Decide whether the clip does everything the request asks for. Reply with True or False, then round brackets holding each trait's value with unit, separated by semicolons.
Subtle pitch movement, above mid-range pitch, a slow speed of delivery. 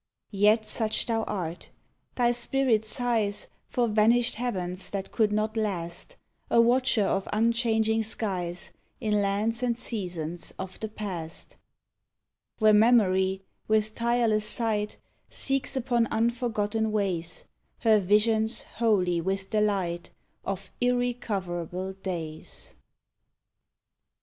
False (3.4 semitones; 215 Hz; 110 wpm)